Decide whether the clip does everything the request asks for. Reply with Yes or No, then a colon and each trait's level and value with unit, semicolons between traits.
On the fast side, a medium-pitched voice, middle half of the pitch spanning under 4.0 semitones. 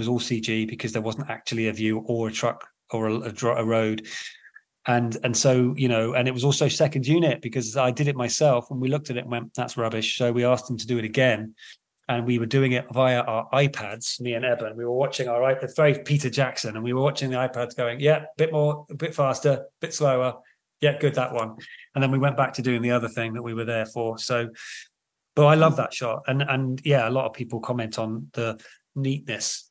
No: fast, 245 wpm; low, 125 Hz; average, 2.9 semitones